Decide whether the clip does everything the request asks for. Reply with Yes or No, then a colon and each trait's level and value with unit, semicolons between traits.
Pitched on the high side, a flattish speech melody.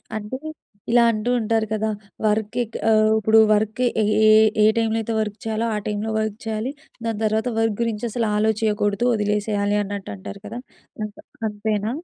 Yes: high, 215 Hz; narrow, 1.2 semitones